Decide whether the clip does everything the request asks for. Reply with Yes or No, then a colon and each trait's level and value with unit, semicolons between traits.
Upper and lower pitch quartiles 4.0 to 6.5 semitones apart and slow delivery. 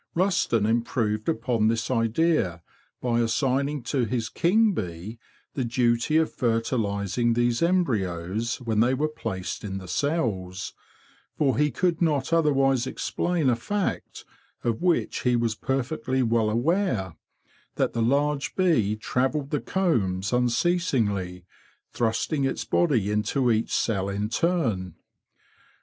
Yes: average, 5.3 semitones; slow, 125 wpm